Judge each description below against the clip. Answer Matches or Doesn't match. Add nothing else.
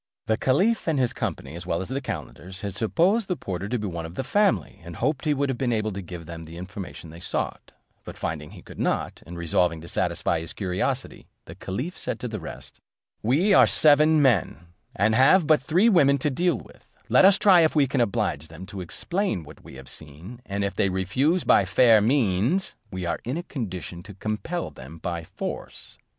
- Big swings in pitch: Matches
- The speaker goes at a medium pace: Doesn't match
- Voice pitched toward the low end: Matches